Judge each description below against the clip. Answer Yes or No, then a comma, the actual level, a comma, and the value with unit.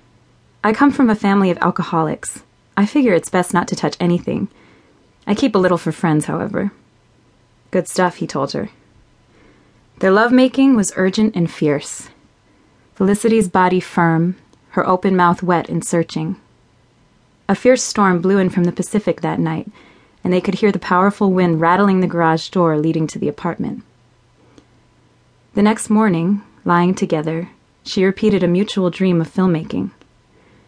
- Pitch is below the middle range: No, medium, 185 Hz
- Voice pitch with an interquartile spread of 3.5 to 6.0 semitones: No, average, 3.1 semitones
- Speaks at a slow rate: No, average, 155 wpm